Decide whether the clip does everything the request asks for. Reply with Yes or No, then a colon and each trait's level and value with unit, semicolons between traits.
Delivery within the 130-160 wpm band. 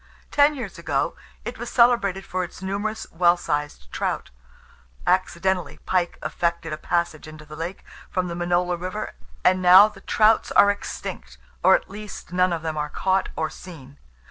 No: average, 170 wpm